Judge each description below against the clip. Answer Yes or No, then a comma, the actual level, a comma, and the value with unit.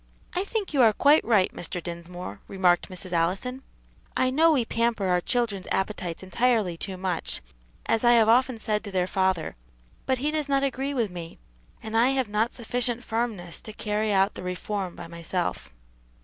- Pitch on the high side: Yes, high, 210 Hz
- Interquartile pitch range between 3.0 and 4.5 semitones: No, average, 5.3 semitones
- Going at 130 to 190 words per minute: Yes, average, 180 wpm